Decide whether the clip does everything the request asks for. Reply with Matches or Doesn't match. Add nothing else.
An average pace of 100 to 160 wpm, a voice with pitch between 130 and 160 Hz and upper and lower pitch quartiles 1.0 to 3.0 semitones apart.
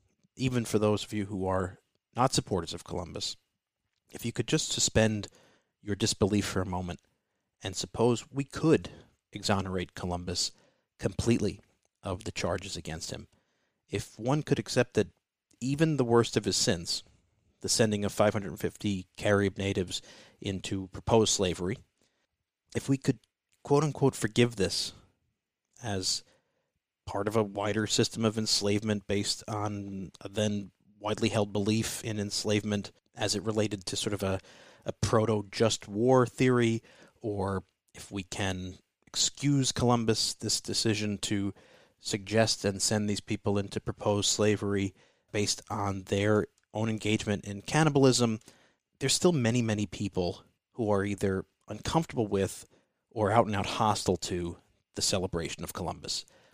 Doesn't match